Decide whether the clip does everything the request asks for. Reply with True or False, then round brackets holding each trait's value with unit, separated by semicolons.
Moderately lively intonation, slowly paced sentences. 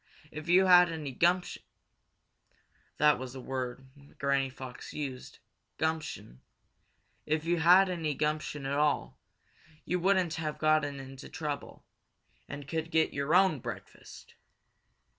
True (3.3 semitones; 125 wpm)